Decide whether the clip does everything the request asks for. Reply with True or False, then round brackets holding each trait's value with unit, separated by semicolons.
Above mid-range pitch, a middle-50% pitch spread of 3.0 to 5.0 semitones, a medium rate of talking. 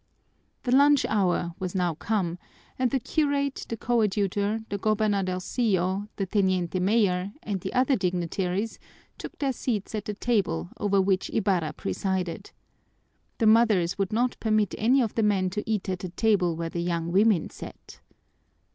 True (200 Hz; 3.5 semitones; 155 wpm)